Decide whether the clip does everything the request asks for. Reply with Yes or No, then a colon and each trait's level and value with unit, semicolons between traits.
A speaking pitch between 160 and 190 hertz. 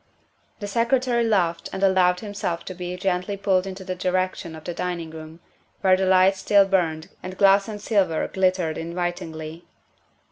Yes: medium, 185 Hz